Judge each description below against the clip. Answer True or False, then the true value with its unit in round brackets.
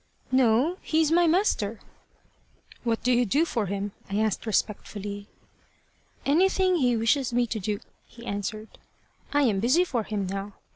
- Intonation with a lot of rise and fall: True (5.7 semitones)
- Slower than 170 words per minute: True (150 wpm)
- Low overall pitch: False (230 Hz)